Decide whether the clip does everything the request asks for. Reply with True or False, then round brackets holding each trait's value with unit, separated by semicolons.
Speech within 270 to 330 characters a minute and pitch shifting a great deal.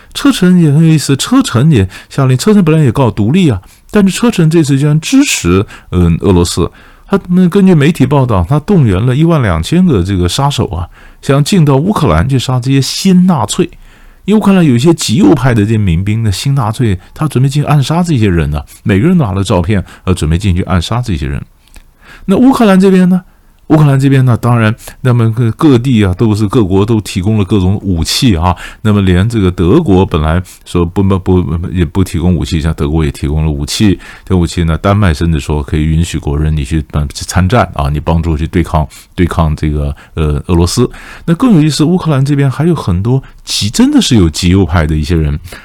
True (315 characters per minute; 8.9 semitones)